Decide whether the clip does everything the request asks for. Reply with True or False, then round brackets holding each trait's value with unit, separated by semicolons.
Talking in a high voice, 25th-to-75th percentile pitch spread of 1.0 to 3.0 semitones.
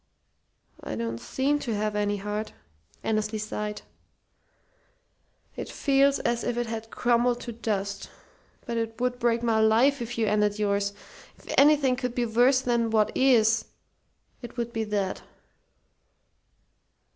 True (230 Hz; 2.5 semitones)